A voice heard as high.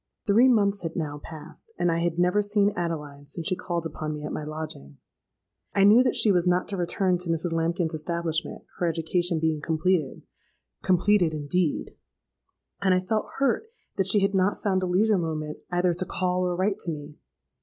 No: medium, 175 Hz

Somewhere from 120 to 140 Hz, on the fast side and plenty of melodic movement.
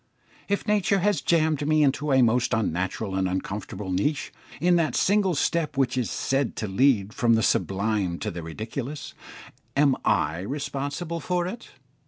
No: low, 135 Hz; average, 160 wpm; wide, 7.3 semitones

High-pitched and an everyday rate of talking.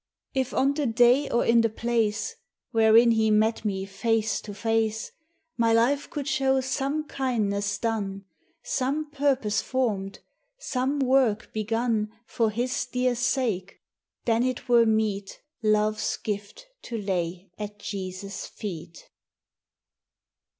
No: high, 225 Hz; slow, 125 wpm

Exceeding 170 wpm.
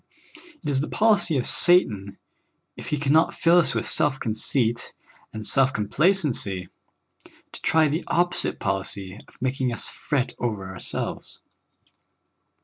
No: average, 140 wpm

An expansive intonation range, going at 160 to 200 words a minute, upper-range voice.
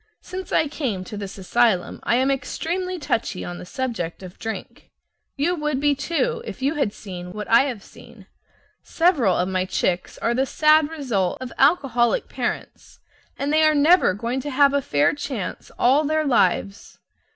Yes: wide, 7.0 semitones; average, 175 wpm; very high, 260 Hz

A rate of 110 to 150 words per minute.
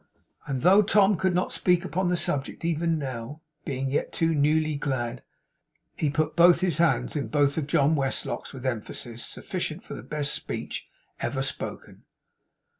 No: average, 160 wpm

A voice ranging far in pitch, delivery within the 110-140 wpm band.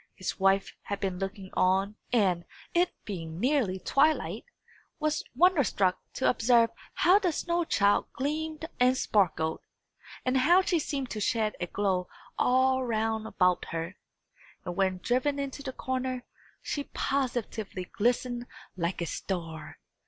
Yes: wide, 6.3 semitones; slow, 135 wpm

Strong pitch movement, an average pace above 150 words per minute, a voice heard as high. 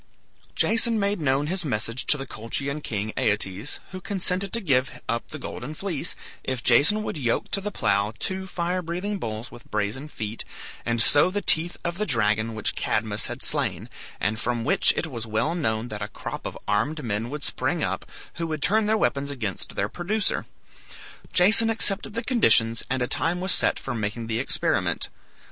No: wide, 8.5 semitones; average, 190 wpm; medium, 140 Hz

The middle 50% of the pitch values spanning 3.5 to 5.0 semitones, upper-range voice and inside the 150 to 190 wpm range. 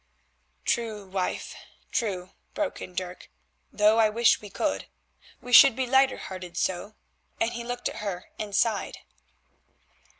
No: average, 4.0 semitones; high, 215 Hz; average, 140 wpm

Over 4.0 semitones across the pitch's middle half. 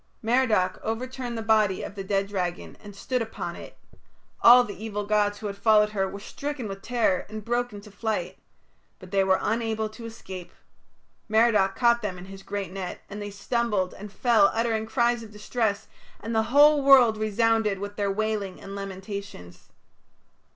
No: narrow, 2.6 semitones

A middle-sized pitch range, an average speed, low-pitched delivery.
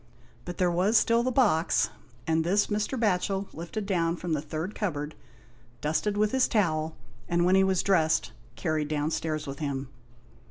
No: average, 4.6 semitones; average, 165 wpm; medium, 175 Hz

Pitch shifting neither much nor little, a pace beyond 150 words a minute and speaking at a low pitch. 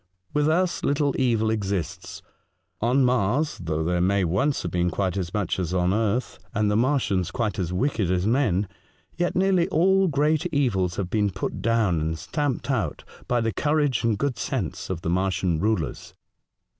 No: wide, 7.2 semitones; average, 175 wpm; low, 110 Hz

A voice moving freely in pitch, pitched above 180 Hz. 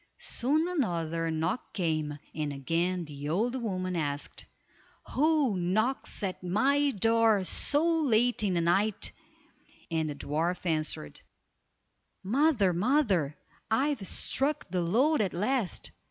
Yes: wide, 7.5 semitones; high, 190 Hz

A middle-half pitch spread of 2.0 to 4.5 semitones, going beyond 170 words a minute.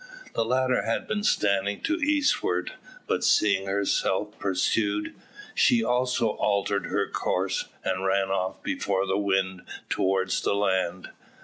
No: average, 3.0 semitones; slow, 135 wpm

